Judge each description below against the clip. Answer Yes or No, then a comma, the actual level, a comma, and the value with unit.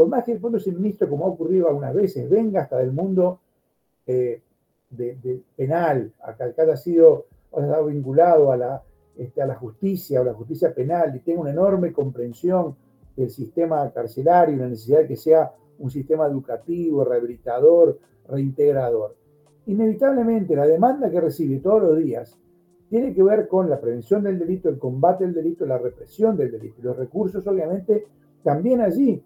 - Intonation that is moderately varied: No, wide, 6.6 semitones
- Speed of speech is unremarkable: Yes, average, 175 wpm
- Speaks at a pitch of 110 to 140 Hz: No, medium, 165 Hz